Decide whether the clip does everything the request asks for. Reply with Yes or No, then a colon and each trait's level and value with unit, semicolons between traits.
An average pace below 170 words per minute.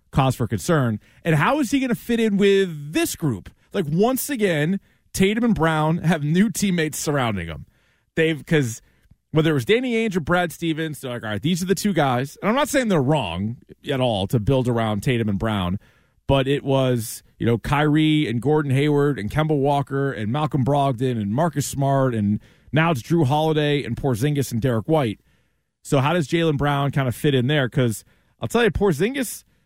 No: fast, 205 wpm